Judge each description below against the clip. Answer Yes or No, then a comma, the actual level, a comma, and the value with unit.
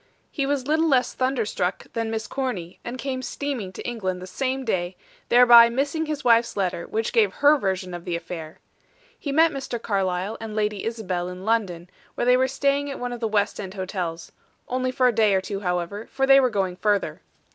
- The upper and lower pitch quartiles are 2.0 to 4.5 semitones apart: No, wide, 5.6 semitones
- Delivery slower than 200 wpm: No, fast, 205 wpm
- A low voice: No, high, 225 Hz